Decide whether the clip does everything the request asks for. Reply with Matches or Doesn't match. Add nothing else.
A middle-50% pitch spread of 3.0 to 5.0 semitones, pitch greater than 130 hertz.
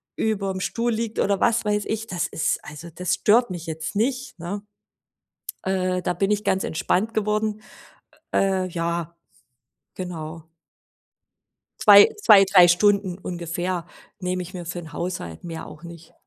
Matches